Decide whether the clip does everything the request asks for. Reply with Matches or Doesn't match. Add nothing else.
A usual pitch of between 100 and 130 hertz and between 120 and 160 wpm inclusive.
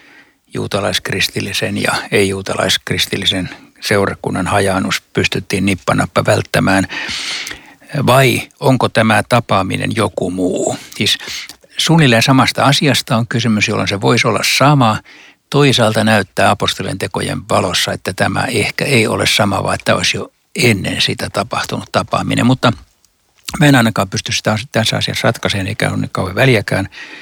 Matches